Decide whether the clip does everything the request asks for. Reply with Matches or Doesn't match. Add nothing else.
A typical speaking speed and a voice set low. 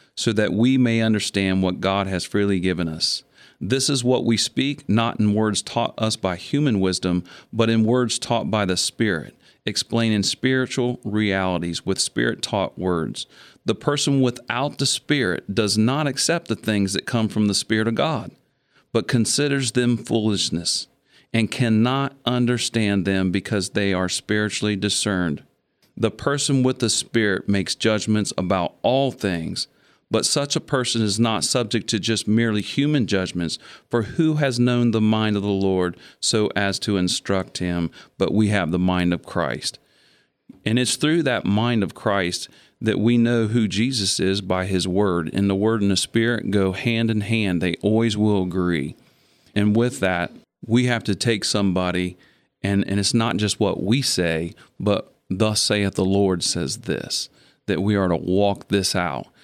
Matches